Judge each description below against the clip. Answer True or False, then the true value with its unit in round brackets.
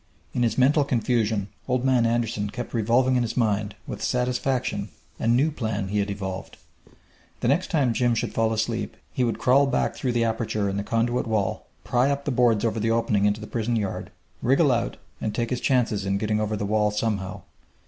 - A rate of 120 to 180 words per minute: False (205 wpm)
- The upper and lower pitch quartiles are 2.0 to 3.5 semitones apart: True (2.8 semitones)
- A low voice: True (115 Hz)